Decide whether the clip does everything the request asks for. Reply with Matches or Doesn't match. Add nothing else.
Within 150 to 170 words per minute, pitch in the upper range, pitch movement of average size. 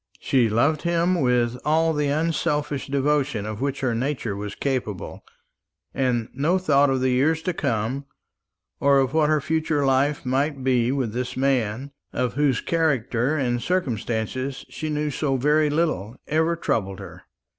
Doesn't match